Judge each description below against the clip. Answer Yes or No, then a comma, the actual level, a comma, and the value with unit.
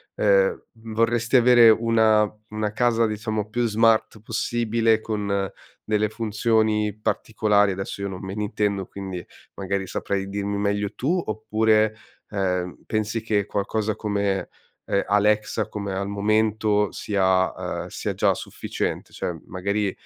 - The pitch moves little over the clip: Yes, narrow, 1.7 semitones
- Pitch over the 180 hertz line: No, low, 105 Hz